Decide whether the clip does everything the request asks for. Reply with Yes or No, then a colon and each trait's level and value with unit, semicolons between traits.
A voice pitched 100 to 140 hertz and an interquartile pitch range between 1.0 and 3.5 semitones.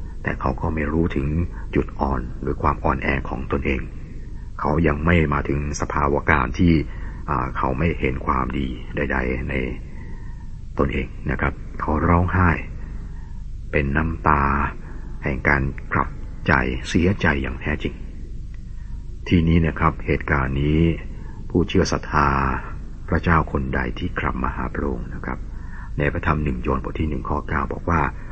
No: very low, 75 Hz; average, 3.2 semitones